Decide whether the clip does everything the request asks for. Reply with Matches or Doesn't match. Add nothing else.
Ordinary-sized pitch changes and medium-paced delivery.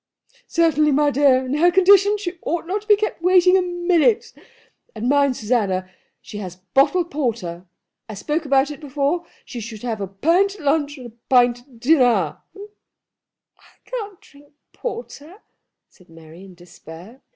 Doesn't match